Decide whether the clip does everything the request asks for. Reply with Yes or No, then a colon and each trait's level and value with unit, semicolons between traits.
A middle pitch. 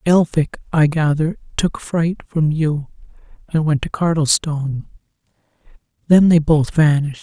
Yes: medium, 155 Hz